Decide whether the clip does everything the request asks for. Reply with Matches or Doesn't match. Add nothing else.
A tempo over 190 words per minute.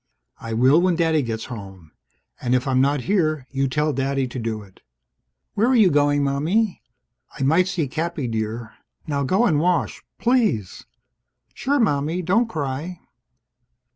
Doesn't match